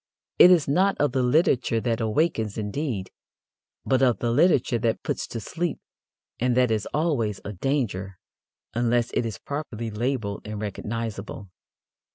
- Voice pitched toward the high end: No, low, 120 Hz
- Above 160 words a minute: No, average, 150 wpm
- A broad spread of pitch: No, average, 4.3 semitones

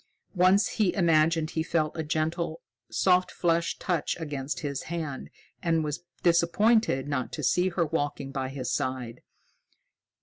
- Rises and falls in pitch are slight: No, average, 3.3 semitones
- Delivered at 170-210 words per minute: No, average, 140 wpm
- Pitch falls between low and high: Yes, medium, 160 Hz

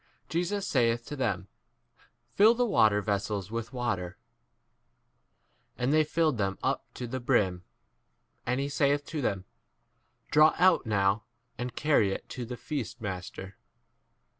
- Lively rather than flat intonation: Yes, wide, 6.4 semitones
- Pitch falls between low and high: No, low, 120 Hz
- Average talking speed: Yes, average, 145 wpm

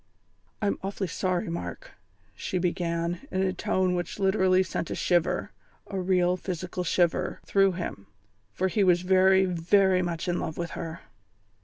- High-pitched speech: No, medium, 180 Hz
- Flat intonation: Yes, narrow, 1.6 semitones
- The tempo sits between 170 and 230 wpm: No, average, 155 wpm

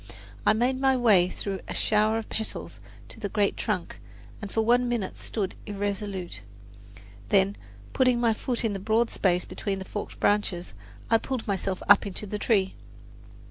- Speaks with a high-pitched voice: Yes, high, 210 Hz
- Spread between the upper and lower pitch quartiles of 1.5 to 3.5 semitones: Yes, average, 2.7 semitones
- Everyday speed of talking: Yes, average, 170 wpm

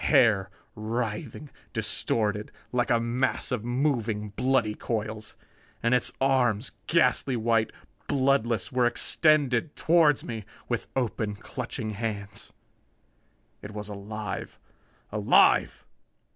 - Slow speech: Yes, slow, 105 wpm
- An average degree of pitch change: Yes, average, 3.0 semitones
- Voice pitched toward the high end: No, low, 115 Hz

